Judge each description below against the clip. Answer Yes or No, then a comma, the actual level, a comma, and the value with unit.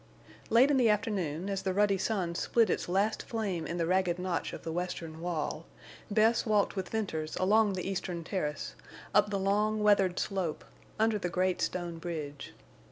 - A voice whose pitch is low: No, high, 190 Hz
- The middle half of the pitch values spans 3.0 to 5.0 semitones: Yes, average, 3.4 semitones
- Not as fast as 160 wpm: No, average, 175 wpm